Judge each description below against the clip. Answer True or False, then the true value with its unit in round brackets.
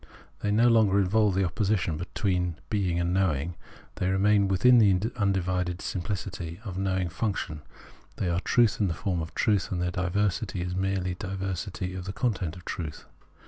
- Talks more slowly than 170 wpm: False (185 wpm)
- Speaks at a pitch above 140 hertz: False (95 Hz)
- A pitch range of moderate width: False (2.2 semitones)